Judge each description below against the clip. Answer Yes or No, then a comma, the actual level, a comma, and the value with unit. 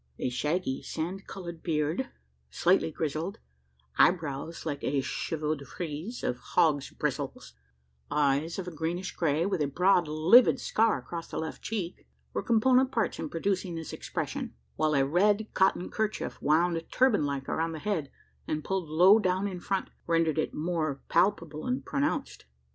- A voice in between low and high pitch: Yes, medium, 170 Hz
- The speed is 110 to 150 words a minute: No, average, 160 wpm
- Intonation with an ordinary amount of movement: Yes, average, 4.1 semitones